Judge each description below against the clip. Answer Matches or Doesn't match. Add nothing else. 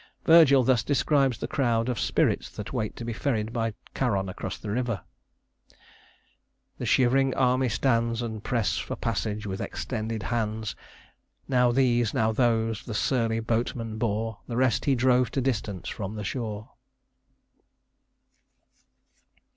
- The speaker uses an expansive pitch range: Doesn't match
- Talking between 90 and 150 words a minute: Matches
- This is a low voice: Matches